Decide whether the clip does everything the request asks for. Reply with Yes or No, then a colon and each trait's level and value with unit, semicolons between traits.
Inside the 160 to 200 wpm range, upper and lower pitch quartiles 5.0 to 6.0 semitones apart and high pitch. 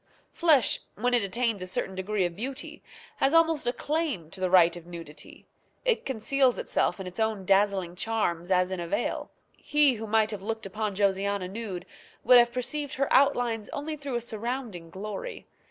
Yes: average, 185 wpm; average, 5.3 semitones; high, 215 Hz